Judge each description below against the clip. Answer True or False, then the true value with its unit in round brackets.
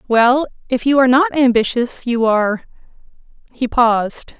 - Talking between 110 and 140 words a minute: True (135 wpm)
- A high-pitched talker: True (250 Hz)